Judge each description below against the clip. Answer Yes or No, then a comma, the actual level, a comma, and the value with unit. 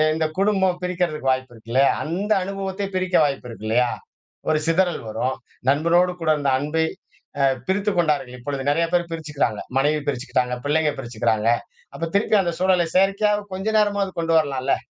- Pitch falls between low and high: Yes, medium, 160 Hz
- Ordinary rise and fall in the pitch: No, wide, 5.7 semitones